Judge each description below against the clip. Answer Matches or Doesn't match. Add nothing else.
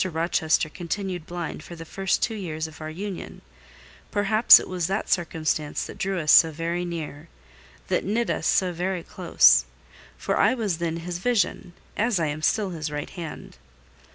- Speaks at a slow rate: Doesn't match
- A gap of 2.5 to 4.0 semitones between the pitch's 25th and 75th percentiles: Matches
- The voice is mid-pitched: Matches